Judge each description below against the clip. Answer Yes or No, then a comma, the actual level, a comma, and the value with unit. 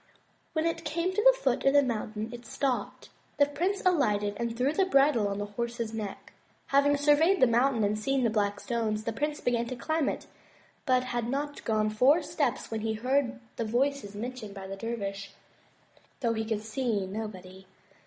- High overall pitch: Yes, high, 240 Hz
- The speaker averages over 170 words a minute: Yes, average, 190 wpm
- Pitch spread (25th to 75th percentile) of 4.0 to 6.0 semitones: Yes, average, 4.8 semitones